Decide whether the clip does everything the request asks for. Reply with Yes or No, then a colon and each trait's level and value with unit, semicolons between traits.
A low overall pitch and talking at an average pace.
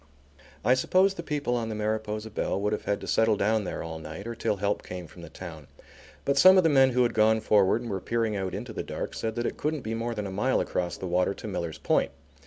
No: low, 110 Hz; fast, 265 wpm